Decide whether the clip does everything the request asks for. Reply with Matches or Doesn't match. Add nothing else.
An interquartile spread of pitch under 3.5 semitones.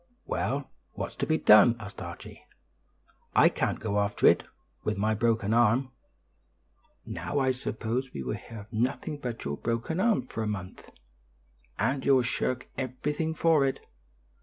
Doesn't match